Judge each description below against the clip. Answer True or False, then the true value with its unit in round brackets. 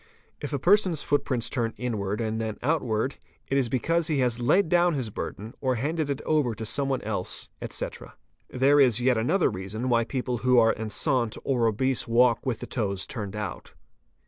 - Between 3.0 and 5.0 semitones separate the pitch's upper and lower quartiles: True (3.8 semitones)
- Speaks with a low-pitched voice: True (125 Hz)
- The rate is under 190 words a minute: False (195 wpm)